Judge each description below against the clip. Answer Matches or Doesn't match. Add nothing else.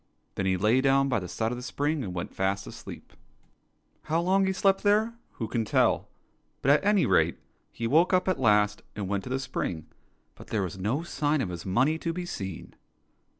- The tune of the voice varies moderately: Doesn't match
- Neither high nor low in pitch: Doesn't match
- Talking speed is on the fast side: Matches